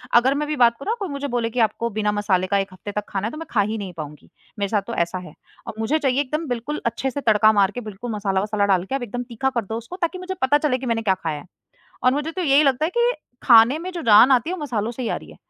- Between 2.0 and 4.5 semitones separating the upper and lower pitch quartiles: No, average, 5.3 semitones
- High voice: Yes, high, 235 Hz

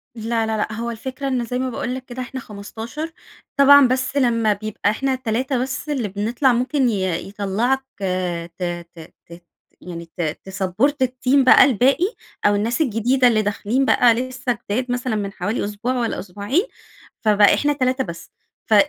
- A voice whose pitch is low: No, high, 240 Hz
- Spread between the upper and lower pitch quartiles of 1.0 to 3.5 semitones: No, average, 3.9 semitones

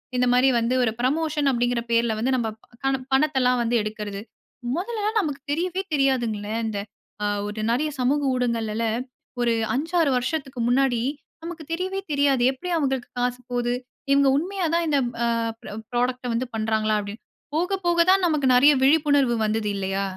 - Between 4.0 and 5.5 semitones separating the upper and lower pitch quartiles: Yes, average, 4.3 semitones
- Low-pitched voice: No, very high, 255 Hz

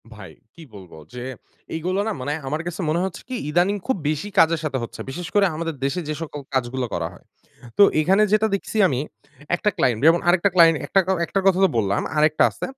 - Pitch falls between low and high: Yes, medium, 165 Hz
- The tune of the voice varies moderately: No, wide, 5.9 semitones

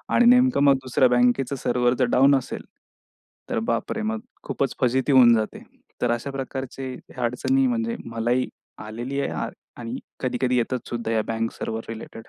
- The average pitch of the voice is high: No, low, 125 Hz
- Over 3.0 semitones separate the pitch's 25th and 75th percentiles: No, narrow, 2.6 semitones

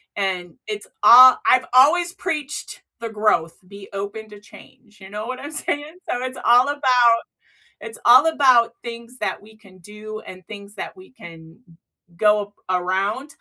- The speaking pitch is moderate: No, high, 220 Hz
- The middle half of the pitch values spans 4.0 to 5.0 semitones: Yes, average, 4.4 semitones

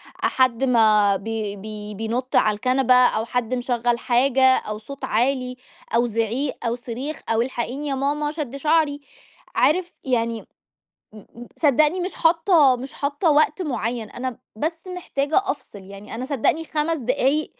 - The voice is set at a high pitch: Yes, very high, 255 Hz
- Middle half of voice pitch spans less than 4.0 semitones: No, average, 4.3 semitones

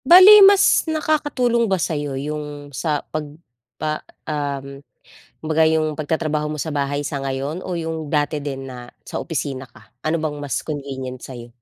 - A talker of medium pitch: Yes, medium, 150 Hz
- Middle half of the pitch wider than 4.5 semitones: No, narrow, 2.4 semitones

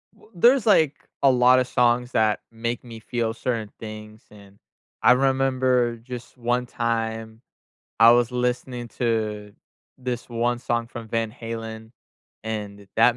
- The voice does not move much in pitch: Yes, narrow, 1.8 semitones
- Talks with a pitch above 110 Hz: Yes, low, 120 Hz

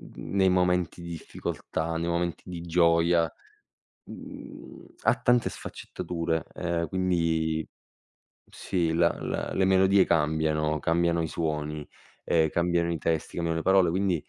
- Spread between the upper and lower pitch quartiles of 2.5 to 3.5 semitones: No, narrow, 1.7 semitones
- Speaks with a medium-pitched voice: No, very low, 85 Hz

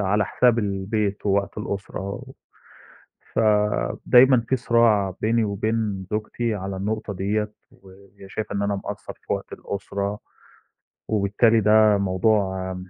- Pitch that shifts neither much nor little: No, narrow, 1.9 semitones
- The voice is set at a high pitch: No, low, 105 Hz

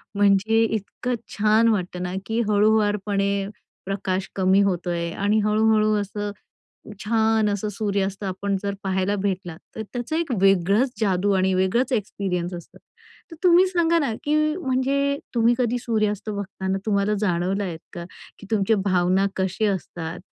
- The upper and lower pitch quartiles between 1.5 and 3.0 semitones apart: Yes, average, 2.7 semitones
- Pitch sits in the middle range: No, high, 205 Hz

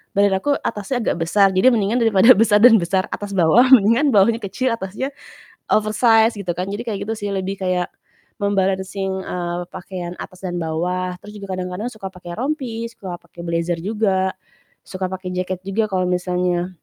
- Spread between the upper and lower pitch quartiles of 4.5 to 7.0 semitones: No, average, 3.0 semitones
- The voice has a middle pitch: No, high, 195 Hz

